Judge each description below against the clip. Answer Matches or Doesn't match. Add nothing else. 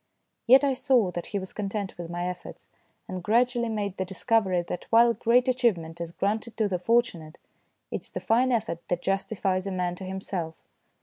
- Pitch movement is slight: Doesn't match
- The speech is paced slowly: Doesn't match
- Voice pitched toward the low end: Doesn't match